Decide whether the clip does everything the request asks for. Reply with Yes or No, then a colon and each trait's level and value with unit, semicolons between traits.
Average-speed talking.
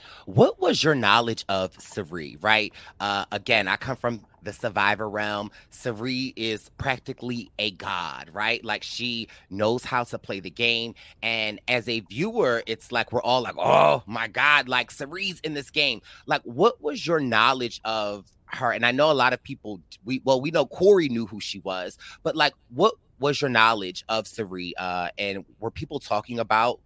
Yes: average, 185 wpm